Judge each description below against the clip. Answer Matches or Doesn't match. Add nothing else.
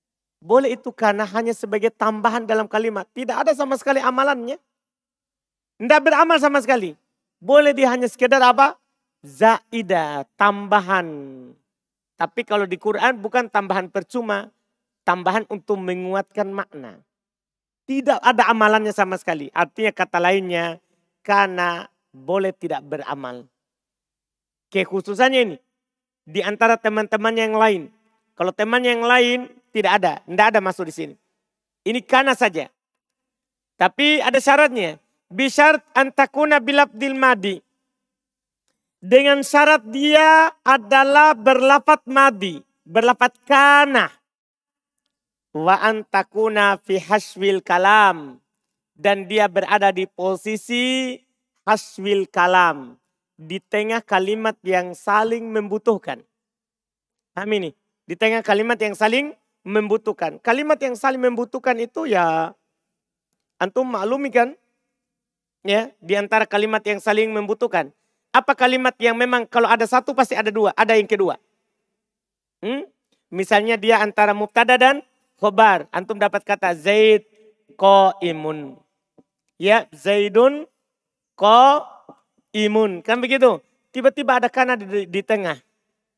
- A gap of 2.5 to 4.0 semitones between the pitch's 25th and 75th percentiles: Doesn't match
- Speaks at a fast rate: Doesn't match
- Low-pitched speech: Doesn't match